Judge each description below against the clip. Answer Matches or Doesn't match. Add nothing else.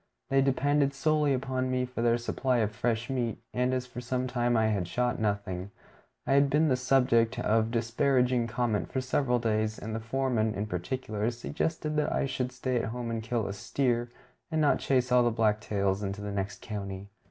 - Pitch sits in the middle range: Doesn't match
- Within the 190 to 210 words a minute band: Matches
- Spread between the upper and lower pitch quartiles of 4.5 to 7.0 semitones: Doesn't match